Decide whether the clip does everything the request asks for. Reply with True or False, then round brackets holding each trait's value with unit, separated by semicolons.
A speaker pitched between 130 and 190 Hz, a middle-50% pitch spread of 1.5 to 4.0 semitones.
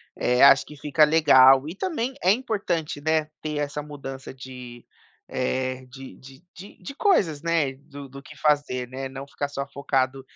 True (140 Hz; 3.1 semitones)